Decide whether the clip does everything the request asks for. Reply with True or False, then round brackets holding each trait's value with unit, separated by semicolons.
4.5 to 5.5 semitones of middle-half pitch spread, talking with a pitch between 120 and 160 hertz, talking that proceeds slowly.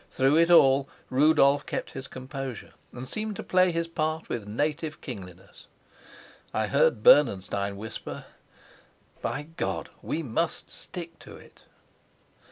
True (5.0 semitones; 140 Hz; 130 wpm)